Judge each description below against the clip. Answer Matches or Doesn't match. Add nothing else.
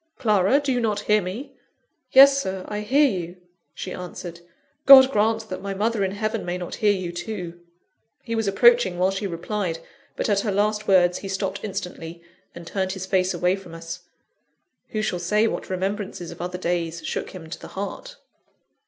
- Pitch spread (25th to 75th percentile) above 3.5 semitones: Doesn't match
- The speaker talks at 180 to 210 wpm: Matches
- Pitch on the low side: Doesn't match